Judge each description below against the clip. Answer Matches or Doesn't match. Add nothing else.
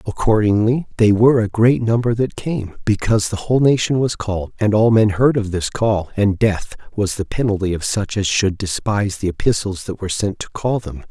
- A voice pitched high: Doesn't match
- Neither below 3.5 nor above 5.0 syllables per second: Doesn't match